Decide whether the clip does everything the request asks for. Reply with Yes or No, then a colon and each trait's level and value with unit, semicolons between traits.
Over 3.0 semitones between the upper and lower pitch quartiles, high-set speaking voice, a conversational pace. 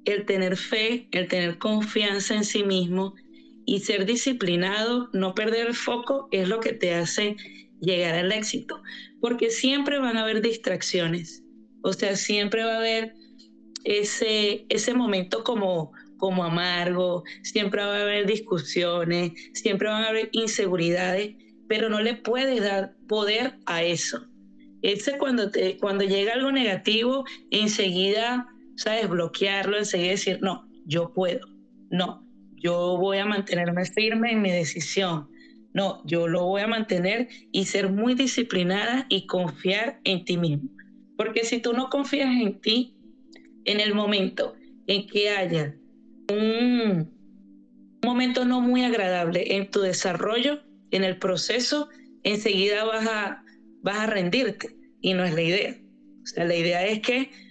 Yes: average, 4.2 semitones; high, 210 Hz; average, 145 wpm